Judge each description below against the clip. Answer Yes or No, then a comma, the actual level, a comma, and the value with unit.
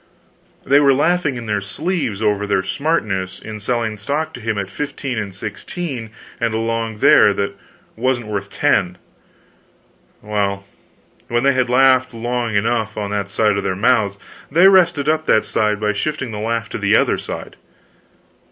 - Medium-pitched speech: No, low, 115 Hz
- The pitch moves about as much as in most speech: Yes, average, 4.3 semitones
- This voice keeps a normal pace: Yes, average, 165 wpm